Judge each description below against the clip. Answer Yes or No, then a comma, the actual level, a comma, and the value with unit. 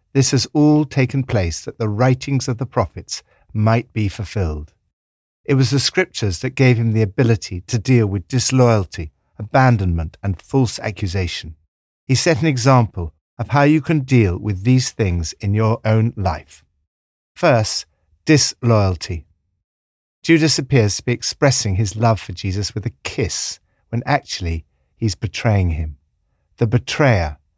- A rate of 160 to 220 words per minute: No, average, 150 wpm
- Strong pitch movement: Yes, wide, 6.8 semitones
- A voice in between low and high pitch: No, low, 110 Hz